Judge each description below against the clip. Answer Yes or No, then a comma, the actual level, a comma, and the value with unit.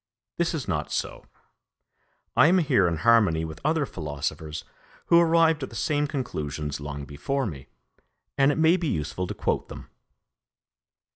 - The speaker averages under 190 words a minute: Yes, average, 155 wpm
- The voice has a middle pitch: No, low, 105 Hz